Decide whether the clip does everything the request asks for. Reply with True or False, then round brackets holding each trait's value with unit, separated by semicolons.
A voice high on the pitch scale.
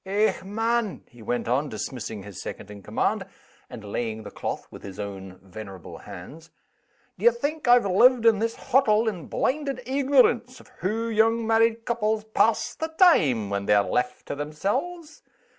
True (210 Hz)